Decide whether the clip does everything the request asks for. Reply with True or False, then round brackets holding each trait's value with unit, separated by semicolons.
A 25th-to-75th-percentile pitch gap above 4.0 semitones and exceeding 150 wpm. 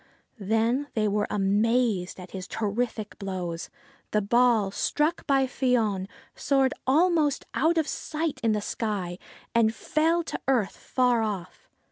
False (5.0 semitones; 135 wpm)